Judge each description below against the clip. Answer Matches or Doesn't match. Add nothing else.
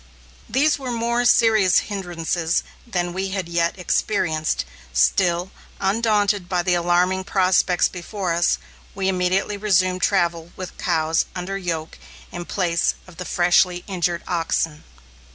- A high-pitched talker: Doesn't match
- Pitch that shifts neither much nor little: Doesn't match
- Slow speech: Matches